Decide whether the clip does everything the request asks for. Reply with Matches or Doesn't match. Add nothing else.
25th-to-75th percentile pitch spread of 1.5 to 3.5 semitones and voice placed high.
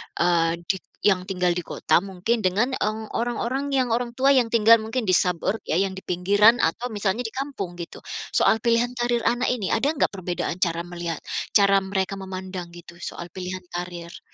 Doesn't match